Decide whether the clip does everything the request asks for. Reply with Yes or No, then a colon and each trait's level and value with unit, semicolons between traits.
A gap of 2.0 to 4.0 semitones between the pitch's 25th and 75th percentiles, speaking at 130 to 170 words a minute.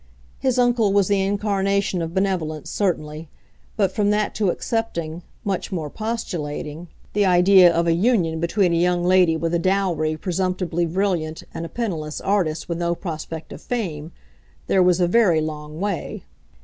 Yes: average, 3.4 semitones; average, 155 wpm